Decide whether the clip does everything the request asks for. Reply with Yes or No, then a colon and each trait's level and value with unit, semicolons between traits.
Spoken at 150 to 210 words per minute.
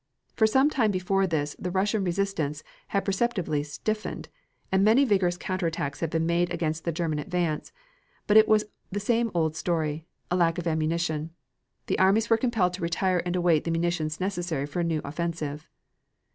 Yes: average, 180 wpm